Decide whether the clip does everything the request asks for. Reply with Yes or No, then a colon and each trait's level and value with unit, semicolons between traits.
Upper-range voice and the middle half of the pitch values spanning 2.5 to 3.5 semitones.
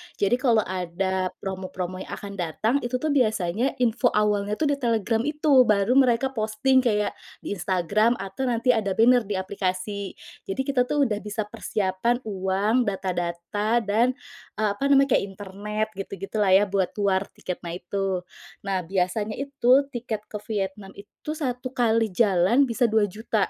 No: high, 210 Hz; average, 4.1 semitones